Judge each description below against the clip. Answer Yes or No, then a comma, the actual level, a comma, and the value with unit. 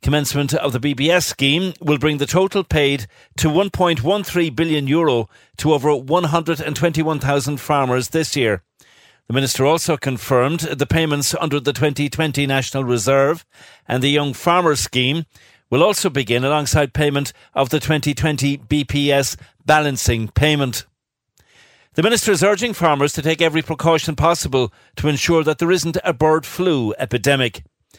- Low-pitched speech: No, medium, 150 Hz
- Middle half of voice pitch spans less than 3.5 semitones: Yes, average, 2.9 semitones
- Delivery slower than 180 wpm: Yes, average, 140 wpm